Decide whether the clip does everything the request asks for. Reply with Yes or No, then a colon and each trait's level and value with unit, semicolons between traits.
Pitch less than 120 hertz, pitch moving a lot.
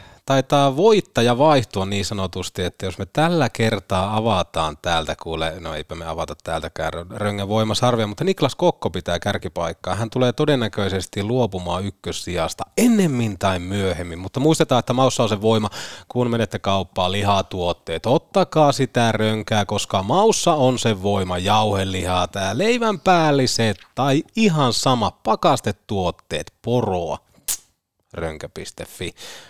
Yes: low, 105 Hz; wide, 5.7 semitones